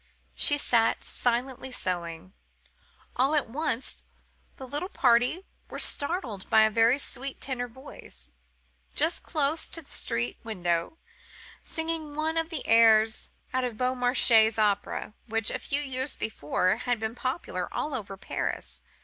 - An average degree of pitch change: Yes, average, 4.6 semitones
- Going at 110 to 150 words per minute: Yes, average, 140 wpm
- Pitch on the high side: Yes, high, 245 Hz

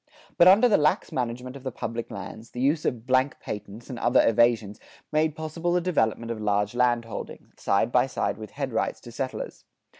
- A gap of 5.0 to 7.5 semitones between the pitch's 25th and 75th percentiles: No, average, 4.0 semitones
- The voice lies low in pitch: Yes, low, 125 Hz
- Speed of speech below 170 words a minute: No, average, 185 wpm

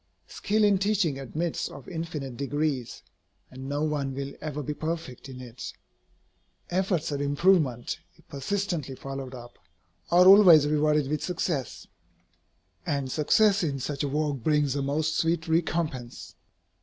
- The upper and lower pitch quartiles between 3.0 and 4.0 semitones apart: Yes, average, 3.5 semitones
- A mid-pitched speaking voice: Yes, medium, 150 Hz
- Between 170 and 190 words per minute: No, average, 140 wpm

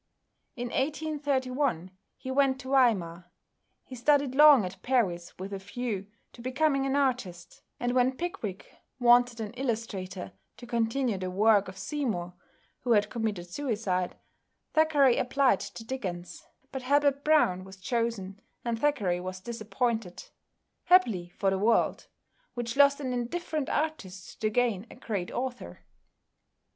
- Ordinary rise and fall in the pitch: No, wide, 5.7 semitones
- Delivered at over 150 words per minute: No, slow, 135 wpm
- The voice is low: No, high, 235 Hz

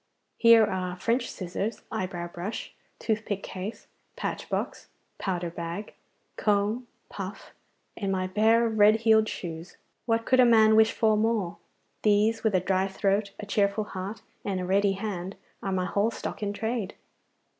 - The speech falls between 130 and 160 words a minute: Yes, average, 155 wpm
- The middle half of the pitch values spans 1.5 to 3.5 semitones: Yes, average, 2.8 semitones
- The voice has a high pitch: Yes, high, 205 Hz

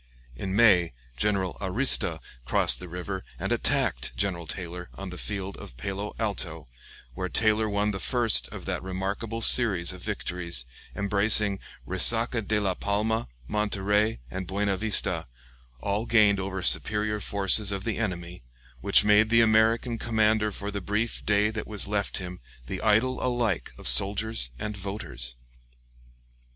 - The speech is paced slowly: No, average, 145 wpm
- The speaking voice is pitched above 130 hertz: No, low, 100 Hz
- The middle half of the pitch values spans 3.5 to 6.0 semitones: No, narrow, 2.6 semitones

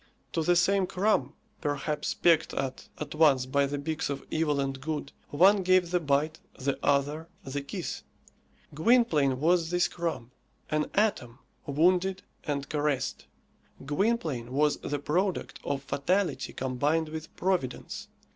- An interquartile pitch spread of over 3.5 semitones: Yes, average, 4.0 semitones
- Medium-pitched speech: Yes, medium, 150 Hz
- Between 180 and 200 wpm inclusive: No, slow, 135 wpm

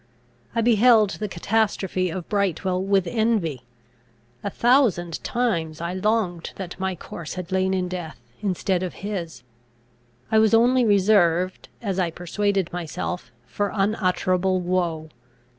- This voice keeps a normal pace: No, slow, 130 wpm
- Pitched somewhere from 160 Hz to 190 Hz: Yes, medium, 185 Hz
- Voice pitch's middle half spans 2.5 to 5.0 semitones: Yes, average, 3.2 semitones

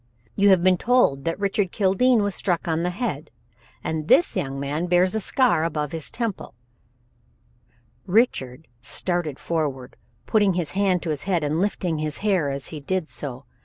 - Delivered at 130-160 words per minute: No, average, 175 wpm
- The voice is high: No, medium, 175 Hz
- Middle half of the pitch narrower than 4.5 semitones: No, average, 4.8 semitones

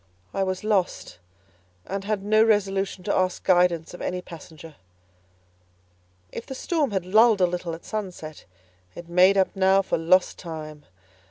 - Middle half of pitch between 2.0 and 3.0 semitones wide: Yes, narrow, 2.5 semitones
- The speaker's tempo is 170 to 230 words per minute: No, average, 155 wpm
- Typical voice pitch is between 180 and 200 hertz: Yes, medium, 185 Hz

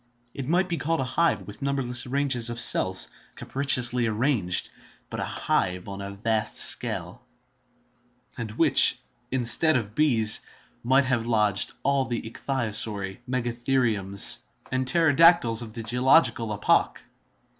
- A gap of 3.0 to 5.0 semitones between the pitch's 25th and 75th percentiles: Yes, average, 4.0 semitones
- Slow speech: Yes, slow, 130 wpm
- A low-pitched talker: Yes, low, 120 Hz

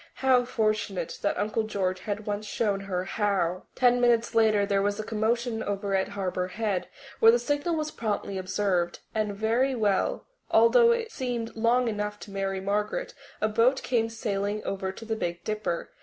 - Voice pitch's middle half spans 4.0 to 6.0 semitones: No, average, 2.9 semitones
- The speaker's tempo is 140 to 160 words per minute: No, average, 175 wpm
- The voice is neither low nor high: No, high, 215 Hz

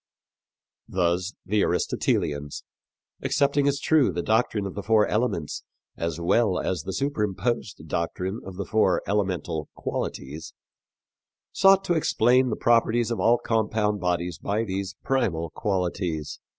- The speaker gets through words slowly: Yes, slow, 130 wpm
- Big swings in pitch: No, average, 4.9 semitones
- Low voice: Yes, low, 100 Hz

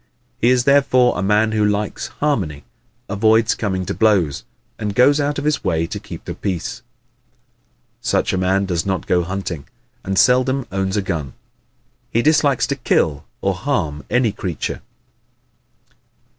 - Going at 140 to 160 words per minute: Yes, average, 155 wpm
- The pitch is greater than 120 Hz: No, low, 105 Hz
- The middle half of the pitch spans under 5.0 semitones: No, average, 5.3 semitones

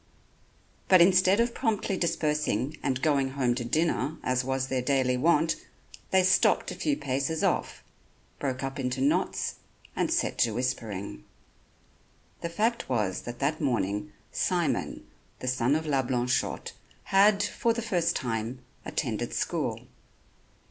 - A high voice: No, low, 135 Hz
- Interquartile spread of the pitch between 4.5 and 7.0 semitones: Yes, average, 5.2 semitones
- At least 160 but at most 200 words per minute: No, average, 140 wpm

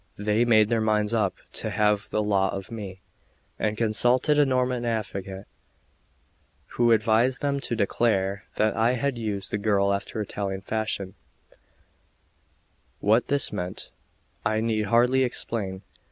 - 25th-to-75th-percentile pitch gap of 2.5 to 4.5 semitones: Yes, average, 2.9 semitones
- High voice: No, low, 110 Hz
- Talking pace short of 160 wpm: Yes, average, 140 wpm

